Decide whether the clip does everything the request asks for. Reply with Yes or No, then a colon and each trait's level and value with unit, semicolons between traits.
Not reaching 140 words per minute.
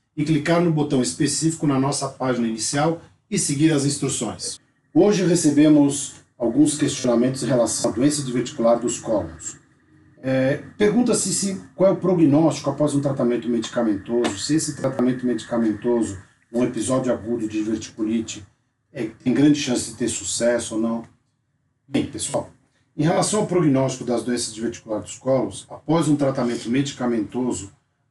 No: average, 150 wpm